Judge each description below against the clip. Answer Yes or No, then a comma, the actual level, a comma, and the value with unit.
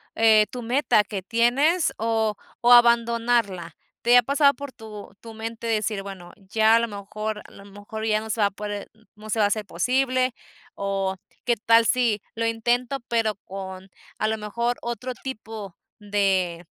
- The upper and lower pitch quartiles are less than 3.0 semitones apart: Yes, narrow, 2.6 semitones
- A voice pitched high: Yes, high, 220 Hz